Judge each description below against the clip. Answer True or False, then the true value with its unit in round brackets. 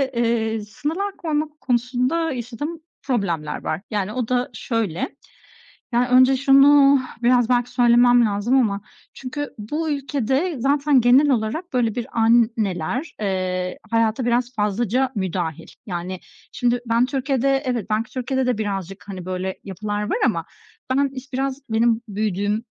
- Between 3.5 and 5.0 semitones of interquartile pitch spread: True (4.2 semitones)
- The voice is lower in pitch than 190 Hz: False (240 Hz)